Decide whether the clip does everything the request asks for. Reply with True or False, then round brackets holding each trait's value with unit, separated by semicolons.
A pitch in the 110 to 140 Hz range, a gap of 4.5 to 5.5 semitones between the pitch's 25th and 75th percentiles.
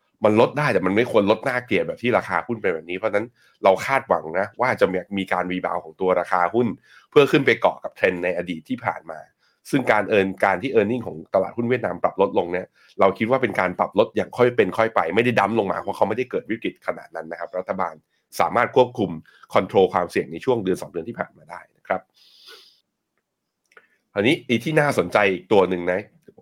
False (100 Hz; 4.9 semitones)